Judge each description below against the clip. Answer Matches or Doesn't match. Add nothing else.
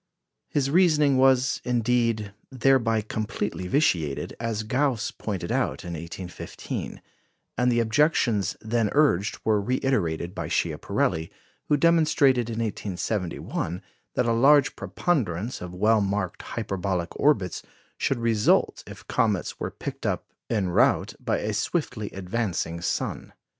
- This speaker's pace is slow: Matches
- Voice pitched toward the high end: Doesn't match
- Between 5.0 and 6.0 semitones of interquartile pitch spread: Matches